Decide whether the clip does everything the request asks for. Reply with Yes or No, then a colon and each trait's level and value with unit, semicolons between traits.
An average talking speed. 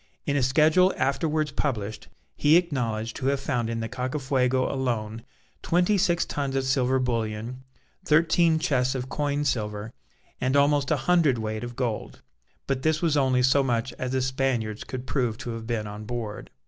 Yes: average, 170 wpm